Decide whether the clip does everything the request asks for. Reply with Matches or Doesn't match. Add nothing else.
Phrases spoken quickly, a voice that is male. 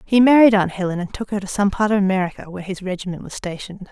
Doesn't match